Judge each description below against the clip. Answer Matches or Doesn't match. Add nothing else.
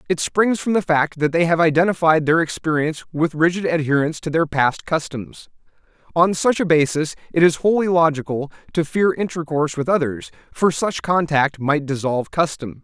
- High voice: Doesn't match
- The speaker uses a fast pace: Doesn't match